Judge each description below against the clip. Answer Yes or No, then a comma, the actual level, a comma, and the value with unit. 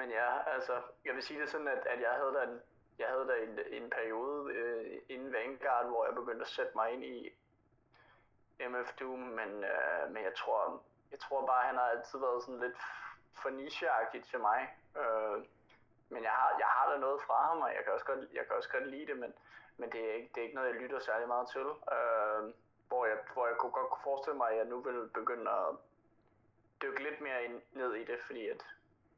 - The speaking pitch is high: No, low, 125 Hz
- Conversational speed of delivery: No, fast, 230 wpm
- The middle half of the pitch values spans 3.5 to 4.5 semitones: Yes, average, 4.1 semitones